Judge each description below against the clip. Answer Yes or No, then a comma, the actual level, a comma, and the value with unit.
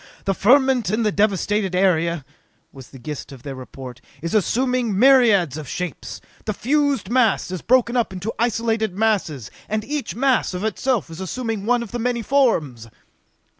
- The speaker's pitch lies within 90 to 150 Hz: No, high, 215 Hz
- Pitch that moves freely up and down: Yes, wide, 6.0 semitones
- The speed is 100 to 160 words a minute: No, average, 170 wpm